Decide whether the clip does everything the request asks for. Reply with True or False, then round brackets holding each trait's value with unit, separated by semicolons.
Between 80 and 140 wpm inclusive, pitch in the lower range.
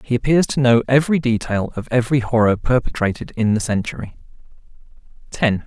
False (150 wpm; 120 Hz)